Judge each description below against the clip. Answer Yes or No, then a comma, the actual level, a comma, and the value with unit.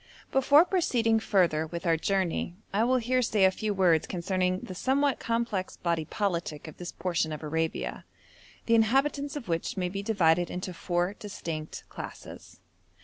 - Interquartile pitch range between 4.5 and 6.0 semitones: Yes, average, 5.2 semitones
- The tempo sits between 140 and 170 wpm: Yes, average, 160 wpm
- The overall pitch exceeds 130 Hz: Yes, high, 190 Hz